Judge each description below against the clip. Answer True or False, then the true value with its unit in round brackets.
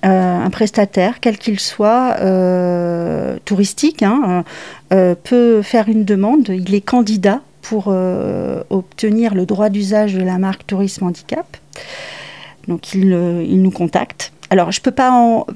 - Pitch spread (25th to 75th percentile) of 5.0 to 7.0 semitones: False (3.3 semitones)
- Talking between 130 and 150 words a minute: True (145 wpm)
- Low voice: False (200 Hz)